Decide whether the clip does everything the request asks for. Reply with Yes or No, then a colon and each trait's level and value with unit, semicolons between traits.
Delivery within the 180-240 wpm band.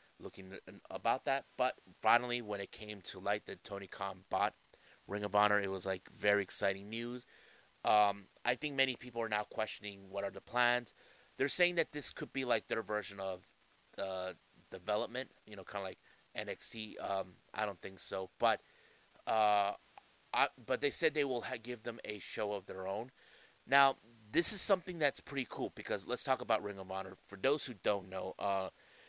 Yes: average, 190 wpm